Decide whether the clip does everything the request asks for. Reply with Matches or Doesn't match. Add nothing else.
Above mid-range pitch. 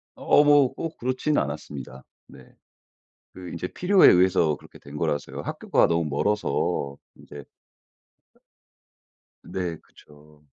Doesn't match